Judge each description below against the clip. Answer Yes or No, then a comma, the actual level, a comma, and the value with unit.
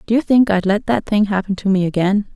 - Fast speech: Yes, fast, 280 wpm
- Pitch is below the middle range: No, high, 205 Hz